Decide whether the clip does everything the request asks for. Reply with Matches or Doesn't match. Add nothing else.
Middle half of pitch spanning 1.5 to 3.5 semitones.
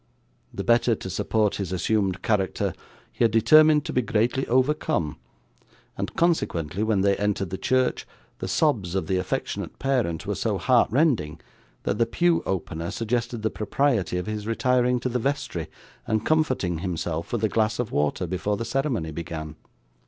Doesn't match